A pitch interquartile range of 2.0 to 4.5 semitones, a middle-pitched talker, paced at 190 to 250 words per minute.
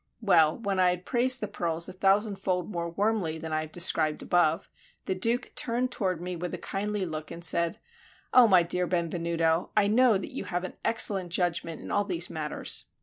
Yes: average, 3.4 semitones; medium, 180 Hz; average, 200 wpm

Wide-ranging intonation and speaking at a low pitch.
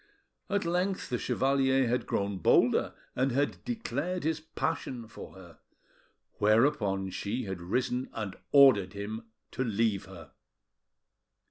Yes: wide, 5.7 semitones; low, 120 Hz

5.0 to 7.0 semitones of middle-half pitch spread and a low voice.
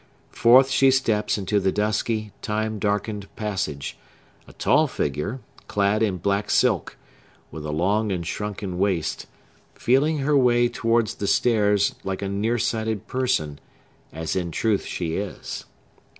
No: average, 3.4 semitones; low, 105 Hz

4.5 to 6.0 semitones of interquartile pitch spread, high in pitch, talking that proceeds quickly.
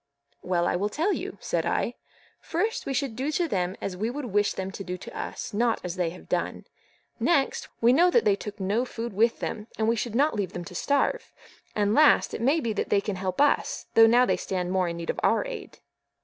Yes: wide, 5.4 semitones; high, 215 Hz; fast, 240 wpm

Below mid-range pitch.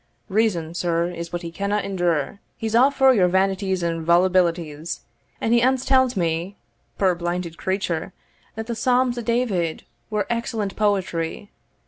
No: high, 190 Hz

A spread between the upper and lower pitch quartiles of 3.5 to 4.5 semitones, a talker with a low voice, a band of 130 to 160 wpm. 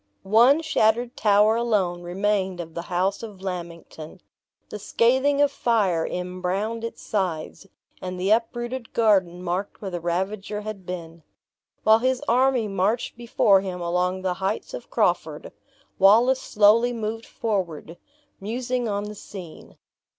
No: average, 4.2 semitones; high, 205 Hz; slow, 135 wpm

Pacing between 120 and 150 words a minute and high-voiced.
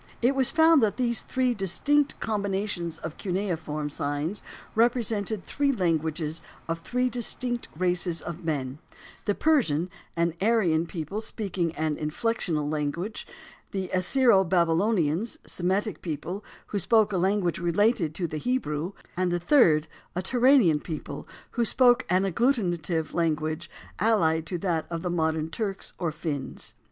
No: average, 140 wpm; medium, 180 Hz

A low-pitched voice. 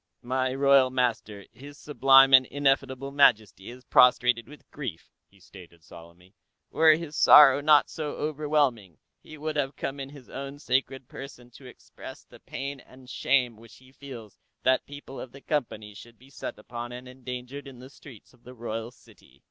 Yes: low, 130 Hz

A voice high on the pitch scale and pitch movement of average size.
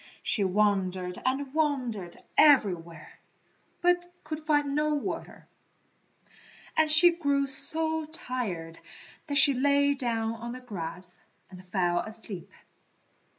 No: very high, 255 Hz; wide, 7.6 semitones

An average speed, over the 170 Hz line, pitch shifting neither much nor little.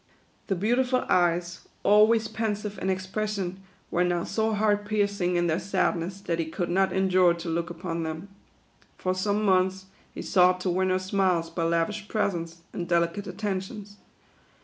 Yes: average, 165 wpm; medium, 185 Hz; average, 3.0 semitones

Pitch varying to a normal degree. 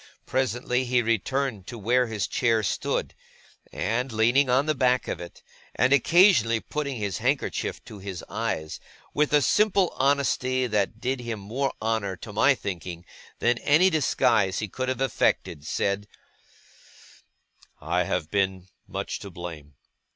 Yes: average, 5.0 semitones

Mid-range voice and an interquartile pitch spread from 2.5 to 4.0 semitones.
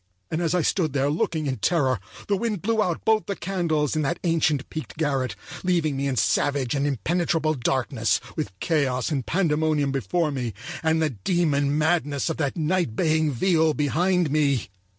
Yes: medium, 155 Hz; average, 3.7 semitones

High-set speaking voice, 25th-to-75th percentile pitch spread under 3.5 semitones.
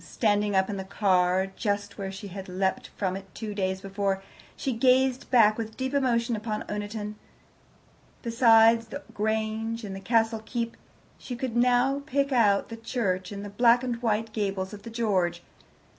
Yes: high, 215 Hz; average, 3.0 semitones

